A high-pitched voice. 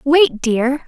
Yes: very high, 270 Hz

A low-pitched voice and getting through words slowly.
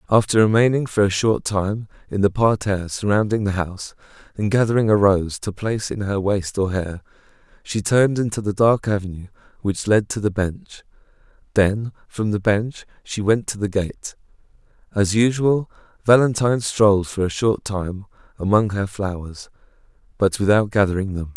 No: low, 105 Hz; average, 165 wpm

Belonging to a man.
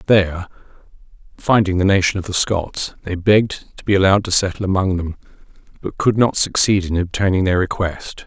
Yes: male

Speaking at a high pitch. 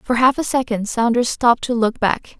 Yes: high, 240 Hz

